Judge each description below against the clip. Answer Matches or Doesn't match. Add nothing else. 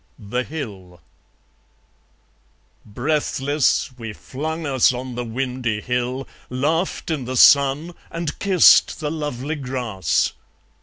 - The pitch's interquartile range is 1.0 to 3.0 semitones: Doesn't match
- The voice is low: Matches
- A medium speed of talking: Doesn't match